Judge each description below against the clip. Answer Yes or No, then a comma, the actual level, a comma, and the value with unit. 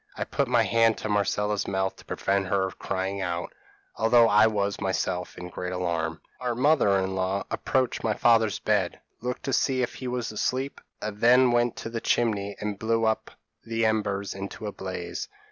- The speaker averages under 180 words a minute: No, average, 185 wpm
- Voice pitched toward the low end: Yes, low, 105 Hz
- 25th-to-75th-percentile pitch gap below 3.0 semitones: No, average, 3.4 semitones